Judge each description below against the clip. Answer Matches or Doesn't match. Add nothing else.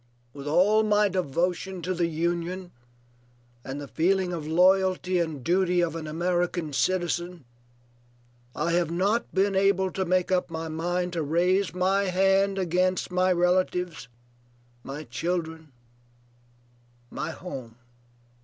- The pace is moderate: Doesn't match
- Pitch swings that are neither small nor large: Doesn't match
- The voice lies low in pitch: Doesn't match